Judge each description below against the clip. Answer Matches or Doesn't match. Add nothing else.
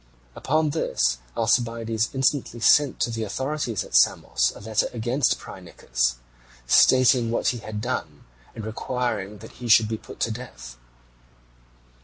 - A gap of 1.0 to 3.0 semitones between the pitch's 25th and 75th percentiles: Matches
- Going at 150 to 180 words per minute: Doesn't match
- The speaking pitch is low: Matches